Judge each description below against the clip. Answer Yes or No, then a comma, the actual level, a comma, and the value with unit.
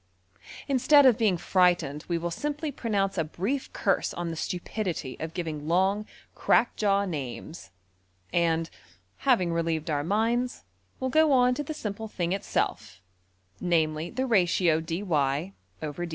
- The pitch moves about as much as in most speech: No, wide, 5.8 semitones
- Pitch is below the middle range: No, medium, 185 Hz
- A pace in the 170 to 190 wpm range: No, slow, 135 wpm